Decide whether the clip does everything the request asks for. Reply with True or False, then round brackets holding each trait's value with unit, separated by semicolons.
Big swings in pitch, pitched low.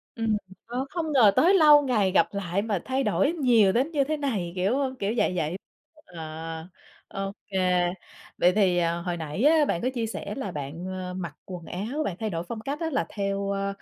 False (6.5 semitones; 200 Hz)